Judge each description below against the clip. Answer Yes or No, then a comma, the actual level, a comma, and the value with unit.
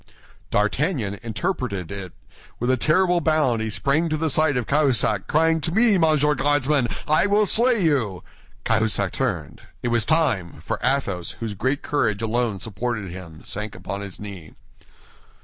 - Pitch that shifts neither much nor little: No, wide, 7.3 semitones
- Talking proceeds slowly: No, average, 155 wpm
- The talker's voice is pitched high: No, low, 125 Hz